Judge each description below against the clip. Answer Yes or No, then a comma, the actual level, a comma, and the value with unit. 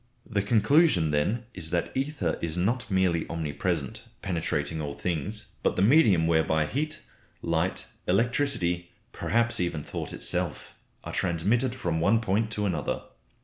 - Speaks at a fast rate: No, average, 140 wpm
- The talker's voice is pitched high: No, very low, 95 Hz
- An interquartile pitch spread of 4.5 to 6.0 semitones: Yes, wide, 5.6 semitones